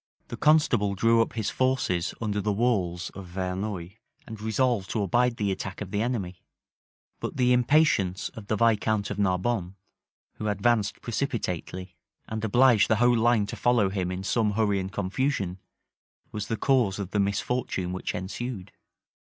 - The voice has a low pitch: Yes, low, 105 Hz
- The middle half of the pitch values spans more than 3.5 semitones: Yes, average, 3.9 semitones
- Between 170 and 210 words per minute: No, average, 160 wpm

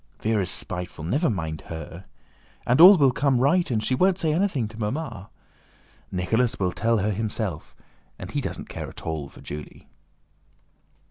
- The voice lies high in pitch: No, low, 110 Hz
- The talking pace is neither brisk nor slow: Yes, average, 160 wpm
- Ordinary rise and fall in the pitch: No, wide, 7.5 semitones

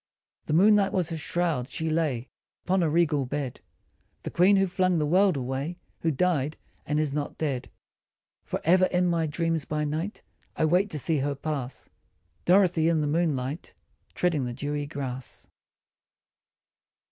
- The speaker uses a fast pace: No, average, 160 wpm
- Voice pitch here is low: No, medium, 155 Hz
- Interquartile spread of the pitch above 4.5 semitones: No, average, 3.5 semitones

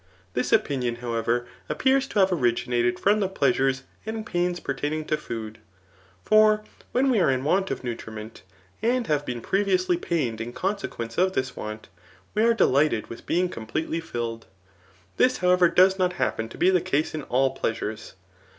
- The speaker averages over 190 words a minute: No, average, 170 wpm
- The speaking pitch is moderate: Yes, medium, 155 Hz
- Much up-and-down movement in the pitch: Yes, wide, 7.9 semitones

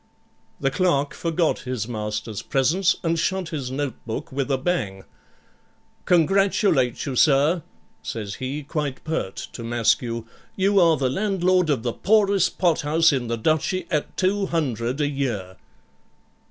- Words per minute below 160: Yes, slow, 135 wpm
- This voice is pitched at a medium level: Yes, medium, 145 Hz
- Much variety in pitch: Yes, wide, 6.0 semitones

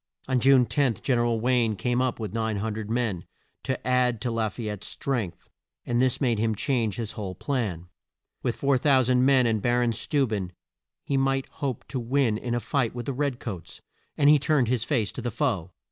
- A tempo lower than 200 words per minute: No, fast, 205 wpm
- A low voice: Yes, low, 120 Hz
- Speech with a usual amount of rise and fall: Yes, average, 3.0 semitones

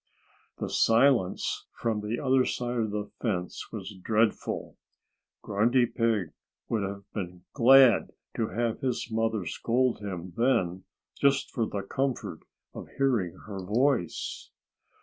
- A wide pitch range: No, average, 3.7 semitones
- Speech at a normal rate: No, slow, 130 wpm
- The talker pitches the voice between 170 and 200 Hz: No, low, 110 Hz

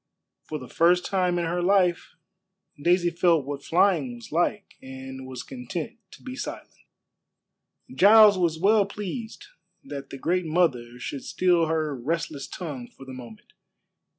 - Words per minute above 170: No, average, 150 wpm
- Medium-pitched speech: Yes, medium, 165 Hz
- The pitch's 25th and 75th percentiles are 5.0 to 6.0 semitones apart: Yes, average, 5.3 semitones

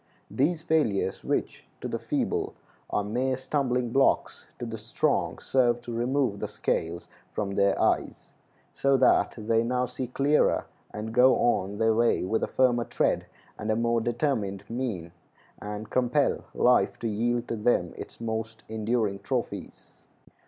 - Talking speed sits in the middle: Yes, average, 150 wpm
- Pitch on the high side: No, low, 115 Hz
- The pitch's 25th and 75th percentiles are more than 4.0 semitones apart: No, average, 3.0 semitones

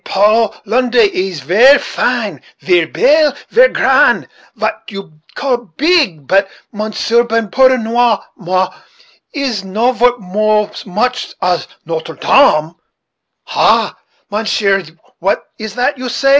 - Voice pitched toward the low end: No, high, 215 Hz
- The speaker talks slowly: Yes, slow, 125 wpm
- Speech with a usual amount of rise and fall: Yes, average, 4.5 semitones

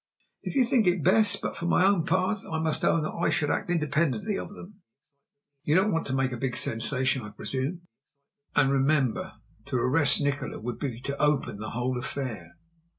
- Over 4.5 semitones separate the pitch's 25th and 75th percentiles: Yes, wide, 5.4 semitones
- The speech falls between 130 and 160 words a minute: No, average, 190 wpm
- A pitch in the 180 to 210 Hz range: No, medium, 145 Hz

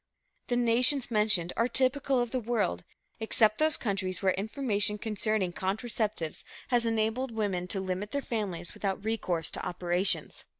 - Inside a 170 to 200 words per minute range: No, average, 145 wpm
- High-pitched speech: Yes, high, 215 Hz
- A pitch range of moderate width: Yes, average, 4.0 semitones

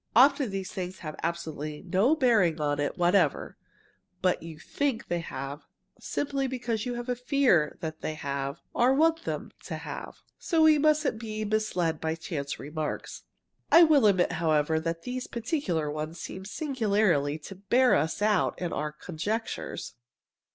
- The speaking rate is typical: Yes, average, 150 wpm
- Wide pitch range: Yes, wide, 7.7 semitones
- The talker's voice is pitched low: No, medium, 185 Hz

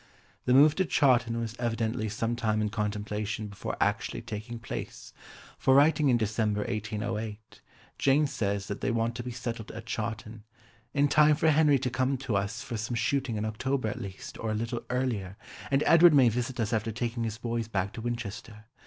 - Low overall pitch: Yes, low, 115 Hz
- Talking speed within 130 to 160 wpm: No, average, 190 wpm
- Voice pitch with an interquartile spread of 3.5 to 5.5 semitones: No, average, 3.0 semitones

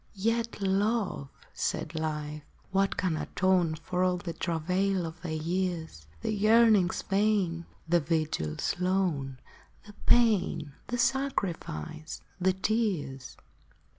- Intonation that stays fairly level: No, average, 4.0 semitones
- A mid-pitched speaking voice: Yes, medium, 180 Hz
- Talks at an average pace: No, slow, 125 wpm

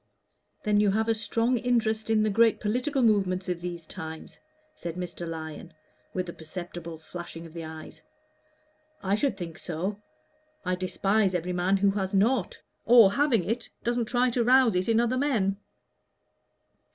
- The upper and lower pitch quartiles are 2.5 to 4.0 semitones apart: No, average, 4.6 semitones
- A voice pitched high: Yes, high, 195 Hz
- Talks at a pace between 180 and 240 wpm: No, average, 165 wpm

